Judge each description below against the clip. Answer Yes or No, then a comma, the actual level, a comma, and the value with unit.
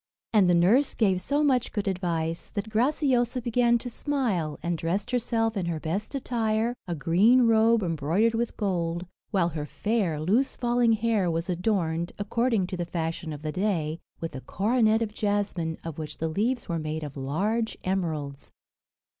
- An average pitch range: No, wide, 5.7 semitones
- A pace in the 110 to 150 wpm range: No, average, 170 wpm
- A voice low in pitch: No, high, 195 Hz